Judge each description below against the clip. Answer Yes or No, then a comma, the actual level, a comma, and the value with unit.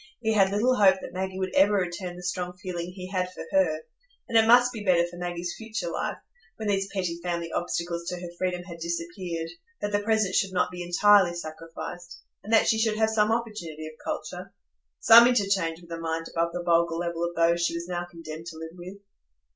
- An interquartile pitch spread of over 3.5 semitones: No, average, 2.9 semitones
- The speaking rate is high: Yes, fast, 210 wpm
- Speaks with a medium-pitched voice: Yes, medium, 180 Hz